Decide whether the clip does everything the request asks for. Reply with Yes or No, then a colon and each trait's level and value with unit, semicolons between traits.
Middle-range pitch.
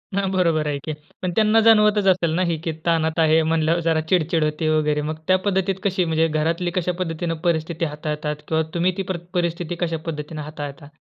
Yes: medium, 165 Hz